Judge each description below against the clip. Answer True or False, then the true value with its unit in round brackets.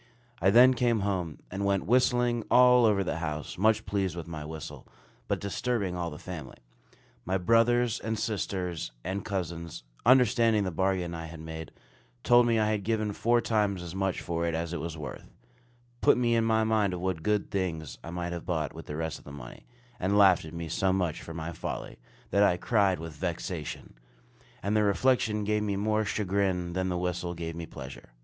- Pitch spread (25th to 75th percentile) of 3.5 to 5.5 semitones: True (4.3 semitones)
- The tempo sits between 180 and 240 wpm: True (200 wpm)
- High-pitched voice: False (95 Hz)